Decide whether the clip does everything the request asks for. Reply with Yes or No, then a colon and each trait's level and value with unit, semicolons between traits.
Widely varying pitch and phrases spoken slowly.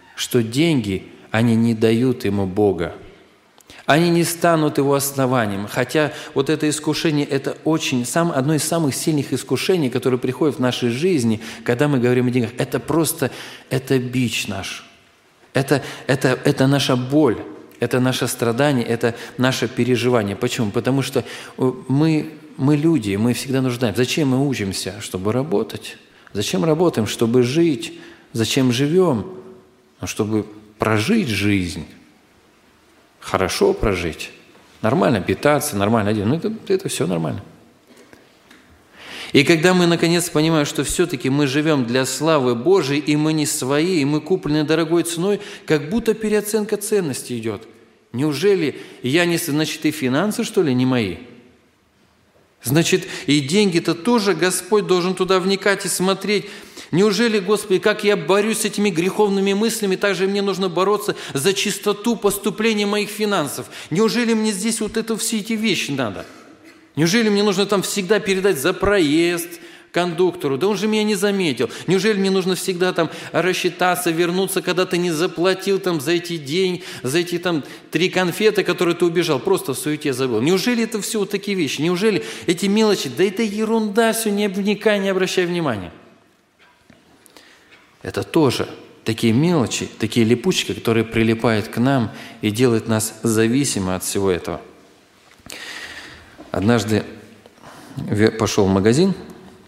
No: wide, 7.5 semitones; average, 145 wpm